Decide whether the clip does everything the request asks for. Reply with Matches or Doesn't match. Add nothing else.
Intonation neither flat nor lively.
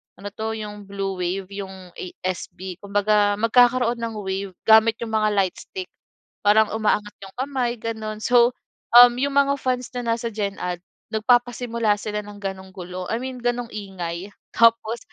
Matches